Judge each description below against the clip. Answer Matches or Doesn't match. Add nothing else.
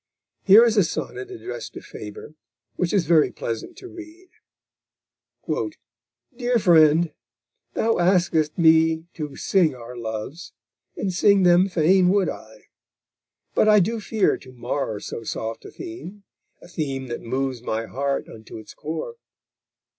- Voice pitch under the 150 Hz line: Doesn't match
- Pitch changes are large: Matches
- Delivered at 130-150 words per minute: Matches